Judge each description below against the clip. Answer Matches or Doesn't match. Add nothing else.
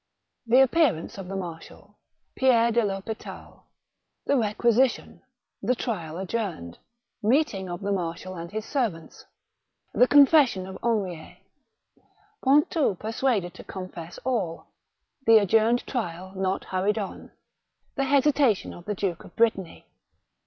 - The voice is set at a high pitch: Matches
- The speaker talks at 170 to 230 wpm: Doesn't match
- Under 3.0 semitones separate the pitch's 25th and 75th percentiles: Doesn't match